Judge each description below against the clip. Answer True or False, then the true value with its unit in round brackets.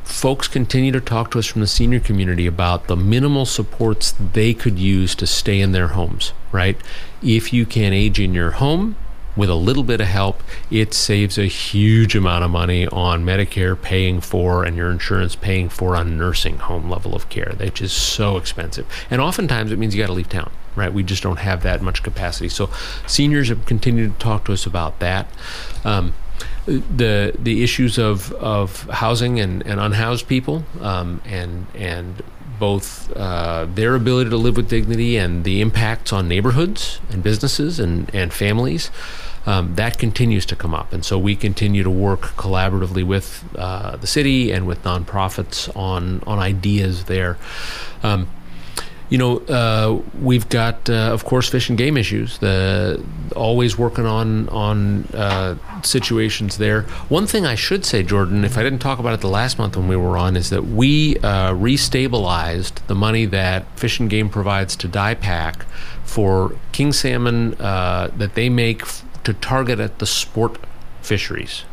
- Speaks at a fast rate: False (180 wpm)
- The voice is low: True (100 Hz)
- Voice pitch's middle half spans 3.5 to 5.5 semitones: True (4.0 semitones)